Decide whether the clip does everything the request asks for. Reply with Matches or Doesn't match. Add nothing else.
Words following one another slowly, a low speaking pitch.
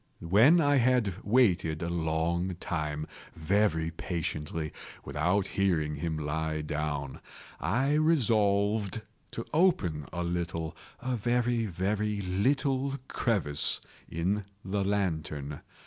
Matches